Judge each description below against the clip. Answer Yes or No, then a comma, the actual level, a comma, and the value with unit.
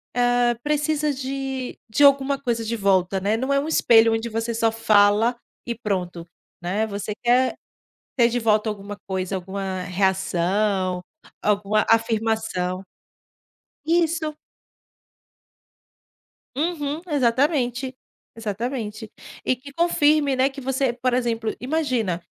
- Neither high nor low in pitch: No, high, 230 Hz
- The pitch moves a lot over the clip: No, average, 4.6 semitones